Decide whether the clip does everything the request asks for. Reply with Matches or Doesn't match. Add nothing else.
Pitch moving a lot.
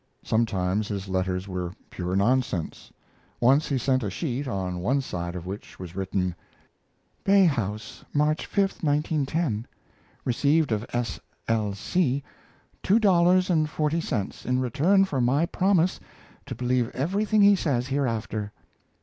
Matches